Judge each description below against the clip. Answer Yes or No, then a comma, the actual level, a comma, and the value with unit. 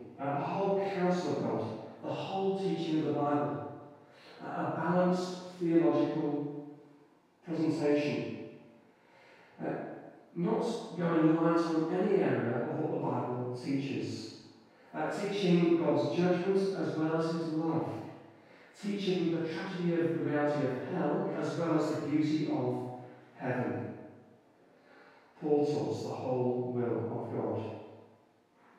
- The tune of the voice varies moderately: Yes, average, 3.1 semitones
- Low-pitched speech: No, medium, 155 Hz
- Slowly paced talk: Yes, slow, 125 wpm